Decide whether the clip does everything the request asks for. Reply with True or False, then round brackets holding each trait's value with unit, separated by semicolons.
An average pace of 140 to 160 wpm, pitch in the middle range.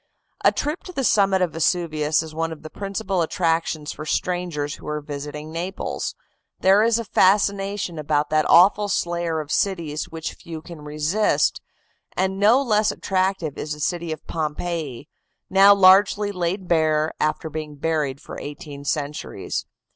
True (155 wpm; 165 Hz)